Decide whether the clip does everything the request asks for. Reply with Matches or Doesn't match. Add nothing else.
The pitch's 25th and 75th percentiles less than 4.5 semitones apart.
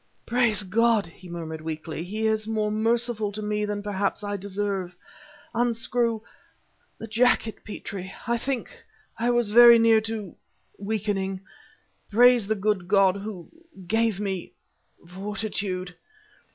Matches